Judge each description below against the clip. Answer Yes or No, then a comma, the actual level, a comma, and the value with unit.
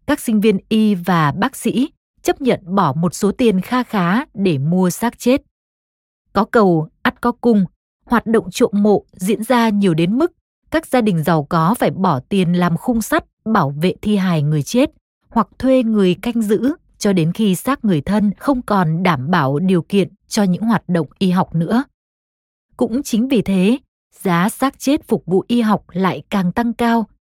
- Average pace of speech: Yes, average, 195 wpm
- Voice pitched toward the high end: Yes, high, 205 Hz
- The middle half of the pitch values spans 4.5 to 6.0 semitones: Yes, average, 4.8 semitones